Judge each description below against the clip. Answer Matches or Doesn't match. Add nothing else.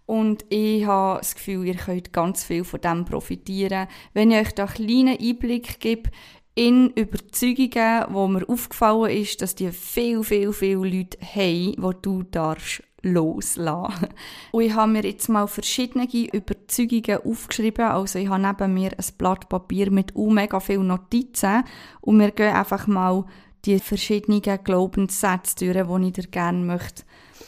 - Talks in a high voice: Matches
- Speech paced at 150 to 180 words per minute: Matches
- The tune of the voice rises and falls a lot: Doesn't match